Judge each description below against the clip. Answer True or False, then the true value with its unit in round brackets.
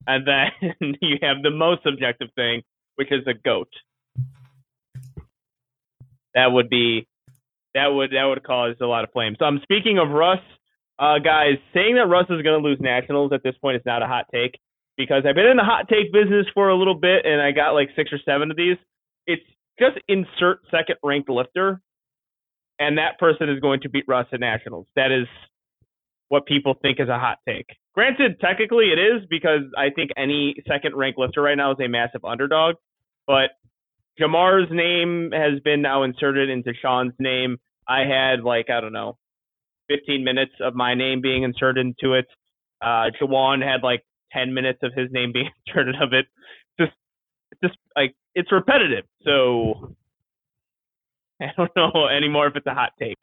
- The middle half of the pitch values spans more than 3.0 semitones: True (3.4 semitones)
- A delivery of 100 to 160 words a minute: False (185 wpm)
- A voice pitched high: False (140 Hz)